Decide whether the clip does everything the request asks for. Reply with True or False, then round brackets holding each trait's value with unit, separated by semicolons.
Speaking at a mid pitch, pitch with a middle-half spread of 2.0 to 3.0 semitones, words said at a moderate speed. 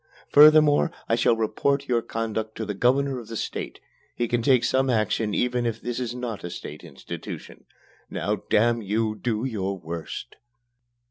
False (115 Hz; 2.7 semitones; 170 wpm)